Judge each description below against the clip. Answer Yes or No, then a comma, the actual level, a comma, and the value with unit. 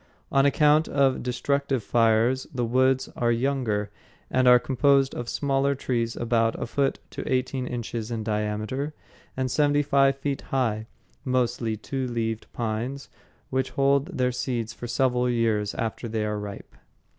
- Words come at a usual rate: Yes, average, 150 wpm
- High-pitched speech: No, low, 125 Hz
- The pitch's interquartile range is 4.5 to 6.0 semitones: No, average, 3.0 semitones